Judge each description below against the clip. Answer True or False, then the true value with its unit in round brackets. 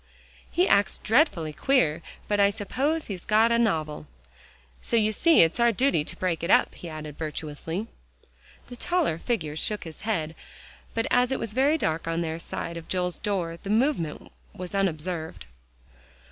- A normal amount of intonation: False (6.3 semitones)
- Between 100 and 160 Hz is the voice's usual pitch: False (190 Hz)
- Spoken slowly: False (170 wpm)